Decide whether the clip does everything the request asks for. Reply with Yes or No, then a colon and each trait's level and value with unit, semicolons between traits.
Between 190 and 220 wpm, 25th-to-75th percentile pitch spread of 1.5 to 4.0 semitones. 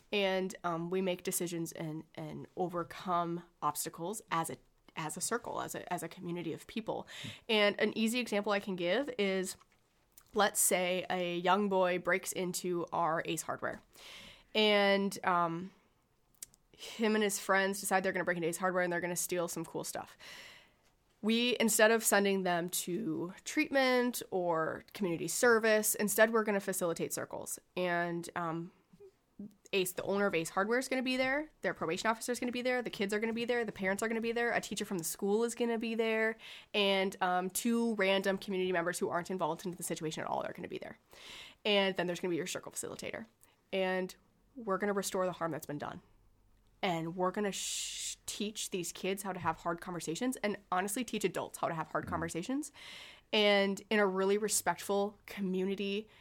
Yes: average, 200 wpm; average, 3.3 semitones